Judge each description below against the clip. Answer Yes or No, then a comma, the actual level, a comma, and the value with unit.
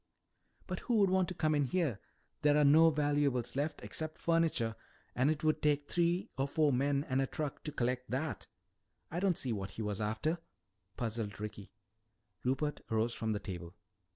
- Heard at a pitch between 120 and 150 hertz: Yes, medium, 140 Hz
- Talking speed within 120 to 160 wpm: No, average, 180 wpm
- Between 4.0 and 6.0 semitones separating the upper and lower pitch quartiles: Yes, wide, 5.4 semitones